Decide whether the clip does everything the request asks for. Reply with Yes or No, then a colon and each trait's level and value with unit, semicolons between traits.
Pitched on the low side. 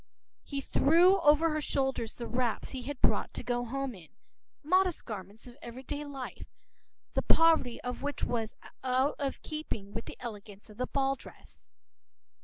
No: very high, 260 Hz